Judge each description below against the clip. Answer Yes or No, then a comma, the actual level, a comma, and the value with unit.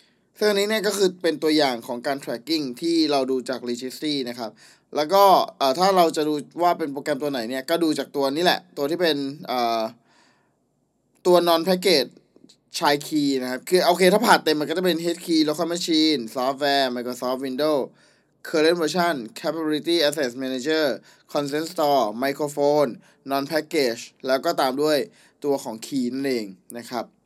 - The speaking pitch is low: No, medium, 150 Hz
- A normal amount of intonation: Yes, average, 4.0 semitones